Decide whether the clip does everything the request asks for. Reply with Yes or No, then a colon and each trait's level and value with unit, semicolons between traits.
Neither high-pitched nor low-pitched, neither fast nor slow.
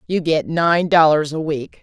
Yes: medium, 160 Hz; average, 195 wpm